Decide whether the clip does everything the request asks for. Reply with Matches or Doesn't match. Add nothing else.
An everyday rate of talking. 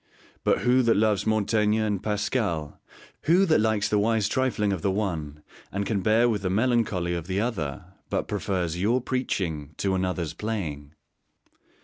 Matches